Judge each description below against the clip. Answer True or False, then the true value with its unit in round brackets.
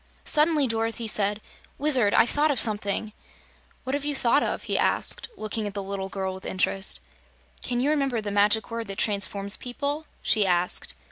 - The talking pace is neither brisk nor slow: True (180 wpm)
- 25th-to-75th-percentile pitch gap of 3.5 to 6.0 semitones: True (4.9 semitones)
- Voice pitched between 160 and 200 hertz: False (220 Hz)